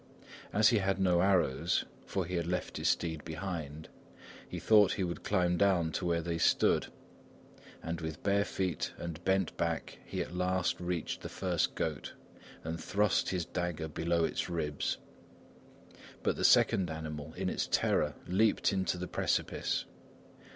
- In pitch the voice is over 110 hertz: No, very low, 85 Hz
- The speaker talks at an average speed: Yes, average, 160 wpm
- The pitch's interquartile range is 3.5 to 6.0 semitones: No, narrow, 2.6 semitones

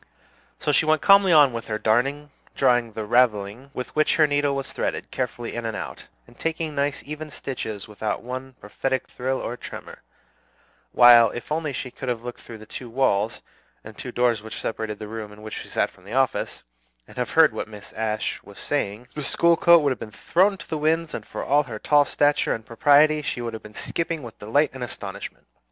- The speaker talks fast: Yes, fast, 215 wpm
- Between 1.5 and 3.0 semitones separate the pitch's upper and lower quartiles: No, average, 4.9 semitones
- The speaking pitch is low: Yes, low, 125 Hz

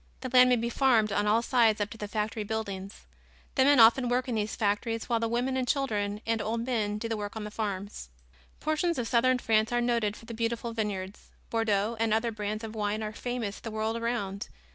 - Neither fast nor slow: No, fast, 225 wpm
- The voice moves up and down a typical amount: No, narrow, 2.2 semitones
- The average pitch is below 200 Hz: No, high, 225 Hz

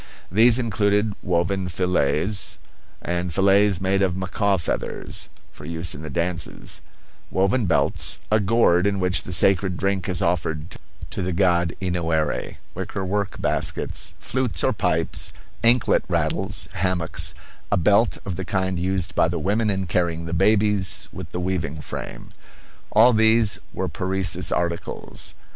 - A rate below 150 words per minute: Yes, average, 140 wpm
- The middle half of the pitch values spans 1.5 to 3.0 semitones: Yes, average, 2.7 semitones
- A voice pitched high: No, very low, 95 Hz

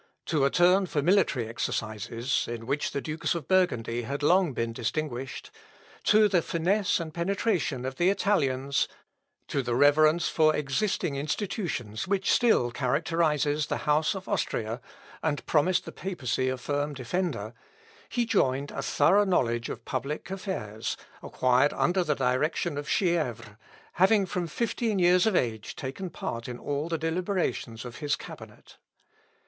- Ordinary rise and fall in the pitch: No, wide, 6.1 semitones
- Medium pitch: Yes, medium, 150 Hz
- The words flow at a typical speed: Yes, average, 150 wpm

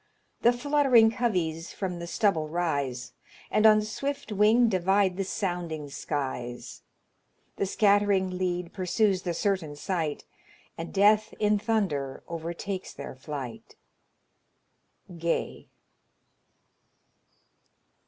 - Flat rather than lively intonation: No, average, 4.6 semitones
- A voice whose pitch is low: No, medium, 185 Hz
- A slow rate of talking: Yes, slow, 100 wpm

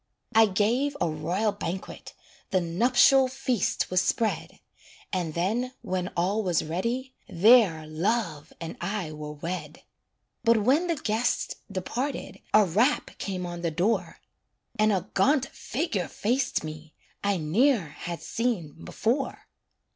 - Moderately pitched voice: No, high, 200 Hz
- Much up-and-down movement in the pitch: Yes, wide, 6.0 semitones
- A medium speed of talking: No, slow, 130 wpm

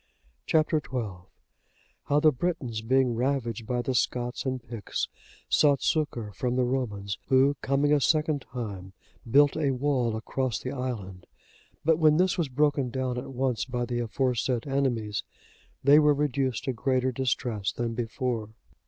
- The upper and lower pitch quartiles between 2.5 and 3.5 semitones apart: Yes, average, 3.1 semitones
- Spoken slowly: No, average, 155 wpm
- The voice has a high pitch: No, low, 130 Hz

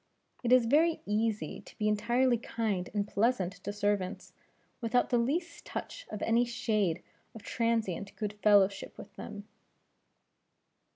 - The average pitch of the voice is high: Yes, high, 220 Hz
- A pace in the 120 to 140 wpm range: Yes, slow, 135 wpm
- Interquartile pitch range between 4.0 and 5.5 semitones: No, average, 2.8 semitones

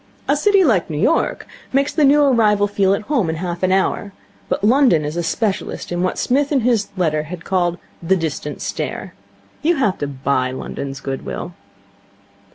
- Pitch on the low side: No, high, 190 Hz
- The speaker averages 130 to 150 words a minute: No, average, 185 wpm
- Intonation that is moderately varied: No, wide, 8.0 semitones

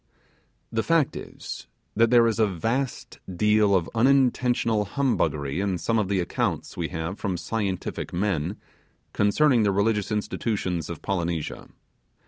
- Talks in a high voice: No, low, 105 Hz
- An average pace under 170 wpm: Yes, slow, 135 wpm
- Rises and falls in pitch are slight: No, average, 4.1 semitones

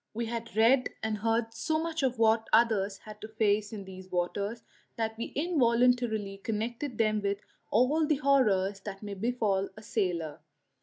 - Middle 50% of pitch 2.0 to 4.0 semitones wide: Yes, average, 2.9 semitones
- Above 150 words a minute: Yes, average, 170 wpm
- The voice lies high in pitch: Yes, high, 220 Hz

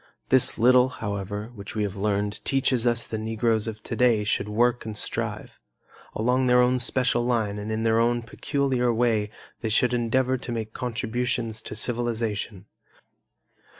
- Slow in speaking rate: No, average, 160 wpm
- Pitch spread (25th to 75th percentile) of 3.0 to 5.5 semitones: No, narrow, 2.4 semitones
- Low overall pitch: Yes, low, 115 Hz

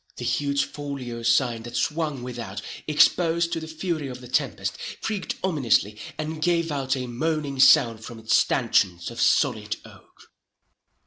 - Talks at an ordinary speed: Yes, average, 150 wpm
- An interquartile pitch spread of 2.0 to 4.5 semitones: No, average, 5.0 semitones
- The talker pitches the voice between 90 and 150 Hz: Yes, low, 135 Hz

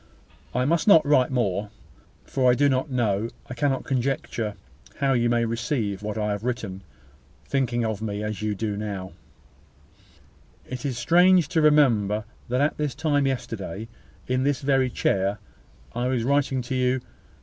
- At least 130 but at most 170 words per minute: Yes, average, 160 wpm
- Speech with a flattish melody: No, average, 4.2 semitones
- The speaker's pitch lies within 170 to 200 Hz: No, low, 125 Hz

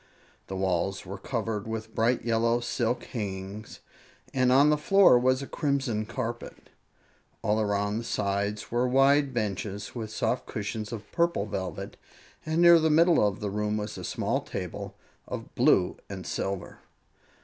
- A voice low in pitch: Yes, low, 110 Hz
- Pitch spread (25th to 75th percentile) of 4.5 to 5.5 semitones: No, average, 3.9 semitones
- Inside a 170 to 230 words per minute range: No, average, 155 wpm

